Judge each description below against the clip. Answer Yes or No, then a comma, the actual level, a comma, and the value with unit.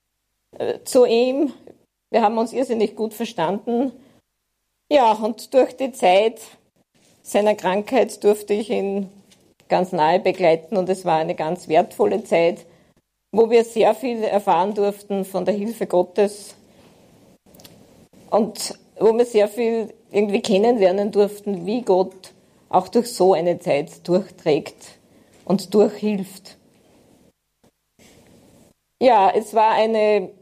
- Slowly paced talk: Yes, slow, 120 wpm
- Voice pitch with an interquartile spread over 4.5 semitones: No, average, 3.3 semitones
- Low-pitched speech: No, high, 205 Hz